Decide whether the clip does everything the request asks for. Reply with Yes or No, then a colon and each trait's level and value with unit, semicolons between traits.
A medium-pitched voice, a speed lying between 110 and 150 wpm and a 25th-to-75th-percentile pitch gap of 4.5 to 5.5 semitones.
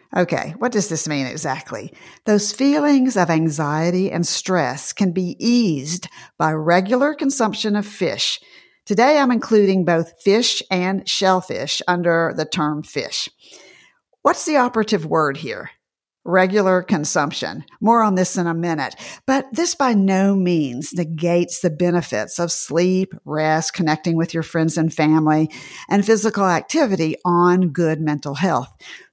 Yes: medium, 180 Hz; average, 140 wpm; average, 4.9 semitones